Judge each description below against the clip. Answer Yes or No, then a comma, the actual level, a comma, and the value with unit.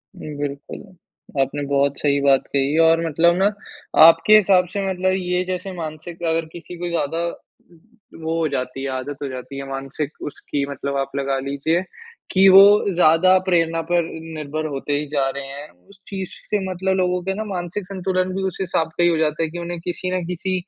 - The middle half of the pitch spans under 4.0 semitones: No, average, 4.3 semitones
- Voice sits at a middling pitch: Yes, medium, 165 Hz